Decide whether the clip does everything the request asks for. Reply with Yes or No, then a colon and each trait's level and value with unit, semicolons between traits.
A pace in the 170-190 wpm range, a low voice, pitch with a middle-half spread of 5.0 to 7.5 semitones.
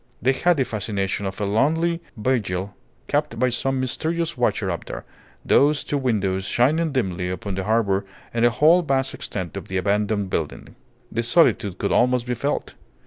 Yes: average, 175 wpm; low, 115 Hz; wide, 5.5 semitones